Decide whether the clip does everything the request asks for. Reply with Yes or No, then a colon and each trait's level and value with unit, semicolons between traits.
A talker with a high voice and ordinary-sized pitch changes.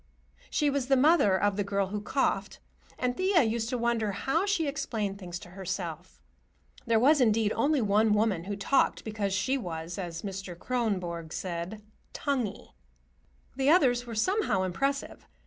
No: high, 215 Hz; wide, 5.7 semitones